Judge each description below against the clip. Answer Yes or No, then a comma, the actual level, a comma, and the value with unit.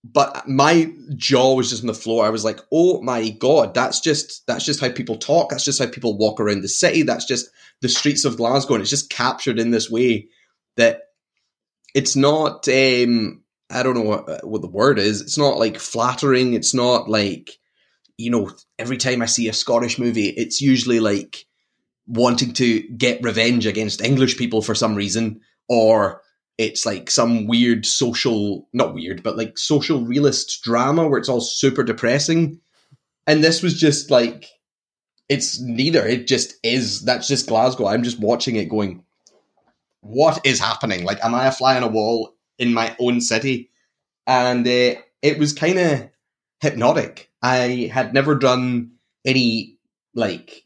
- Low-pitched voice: Yes, low, 125 Hz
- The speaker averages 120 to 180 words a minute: Yes, average, 175 wpm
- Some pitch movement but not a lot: Yes, average, 3.2 semitones